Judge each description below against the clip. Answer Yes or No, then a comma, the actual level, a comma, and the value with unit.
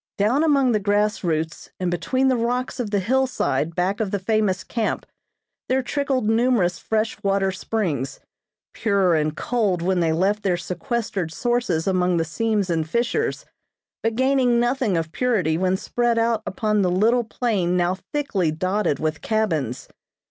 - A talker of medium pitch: No, high, 205 Hz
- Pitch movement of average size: Yes, average, 5.0 semitones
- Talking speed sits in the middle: Yes, average, 160 wpm